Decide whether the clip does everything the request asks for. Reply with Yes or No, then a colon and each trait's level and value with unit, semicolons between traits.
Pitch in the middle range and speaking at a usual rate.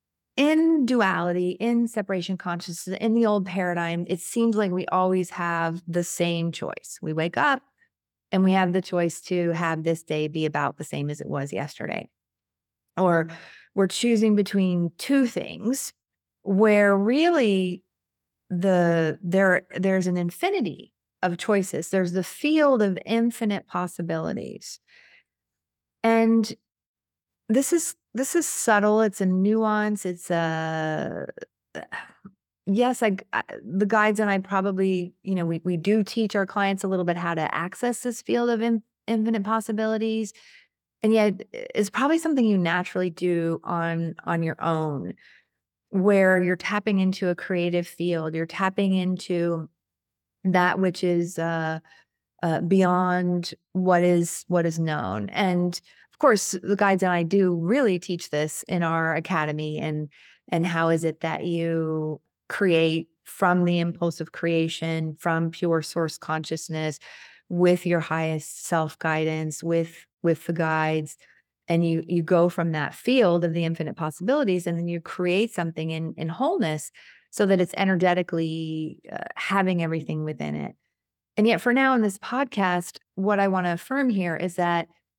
Yes: medium, 180 Hz; average, 150 wpm